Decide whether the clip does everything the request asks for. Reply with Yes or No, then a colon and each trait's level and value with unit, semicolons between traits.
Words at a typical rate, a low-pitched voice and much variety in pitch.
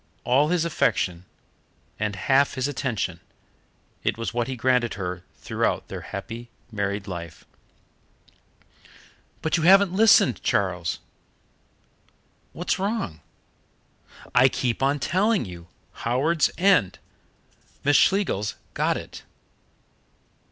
No: slow, 110 wpm; low, 125 Hz; wide, 8.7 semitones